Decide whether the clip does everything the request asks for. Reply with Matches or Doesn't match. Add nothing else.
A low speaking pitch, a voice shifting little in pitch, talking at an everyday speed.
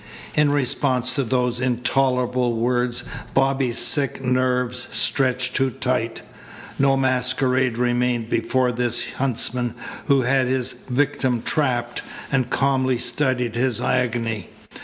Doesn't match